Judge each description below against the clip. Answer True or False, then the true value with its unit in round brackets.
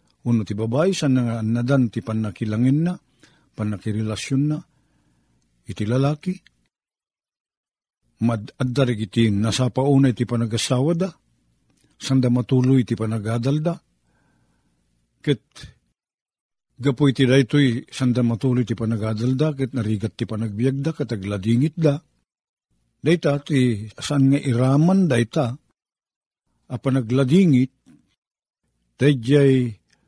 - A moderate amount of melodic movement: True (4.0 semitones)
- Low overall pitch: True (125 Hz)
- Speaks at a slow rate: True (100 wpm)